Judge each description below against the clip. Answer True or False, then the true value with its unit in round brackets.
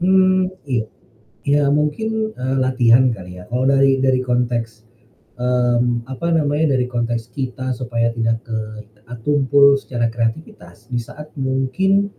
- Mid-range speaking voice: False (130 Hz)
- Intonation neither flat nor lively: True (3.3 semitones)